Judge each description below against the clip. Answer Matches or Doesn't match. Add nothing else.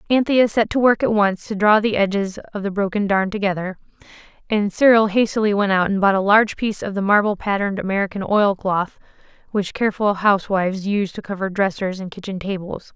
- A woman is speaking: Matches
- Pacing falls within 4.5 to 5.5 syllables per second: Doesn't match